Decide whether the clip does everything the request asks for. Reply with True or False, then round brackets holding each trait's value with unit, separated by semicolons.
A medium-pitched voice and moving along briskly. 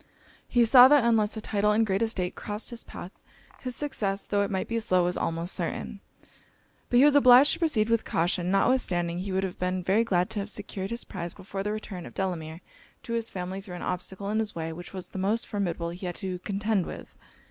False (195 Hz; 225 wpm)